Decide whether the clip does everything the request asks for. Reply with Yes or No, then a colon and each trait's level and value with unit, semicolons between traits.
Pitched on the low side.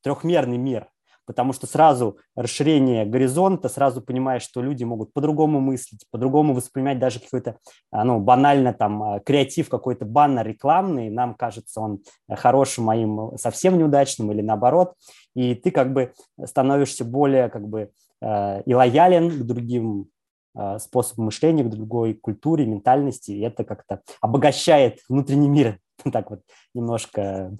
Yes: low, 125 Hz